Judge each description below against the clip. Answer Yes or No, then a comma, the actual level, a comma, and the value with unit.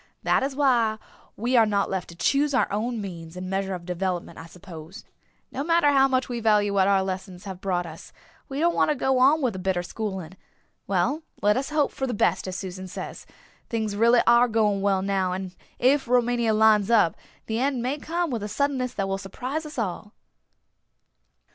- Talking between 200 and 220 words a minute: Yes, fast, 205 wpm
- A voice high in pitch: Yes, high, 215 Hz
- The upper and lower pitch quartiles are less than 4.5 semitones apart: No, average, 5.3 semitones